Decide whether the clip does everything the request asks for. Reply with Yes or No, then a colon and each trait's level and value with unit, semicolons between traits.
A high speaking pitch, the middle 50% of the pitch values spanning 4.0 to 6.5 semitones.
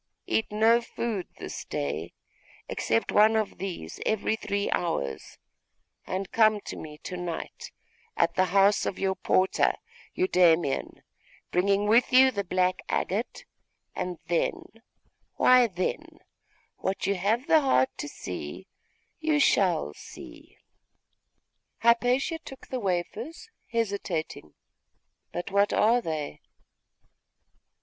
Yes: high, 195 Hz; average, 4.8 semitones